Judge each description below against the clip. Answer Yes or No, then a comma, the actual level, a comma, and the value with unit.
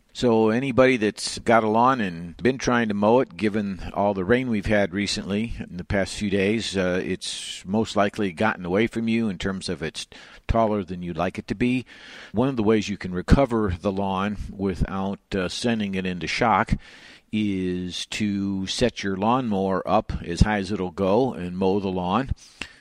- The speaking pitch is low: Yes, low, 100 Hz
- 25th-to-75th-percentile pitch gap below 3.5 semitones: Yes, average, 2.8 semitones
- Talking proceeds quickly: No, average, 195 wpm